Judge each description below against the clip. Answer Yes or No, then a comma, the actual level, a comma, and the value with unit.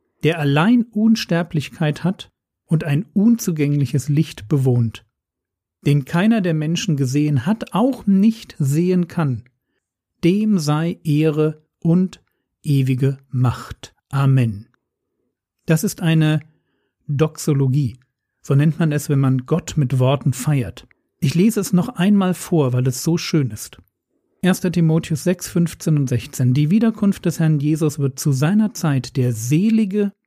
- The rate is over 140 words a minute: No, average, 135 wpm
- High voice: No, medium, 155 Hz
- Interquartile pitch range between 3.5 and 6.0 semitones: Yes, average, 4.6 semitones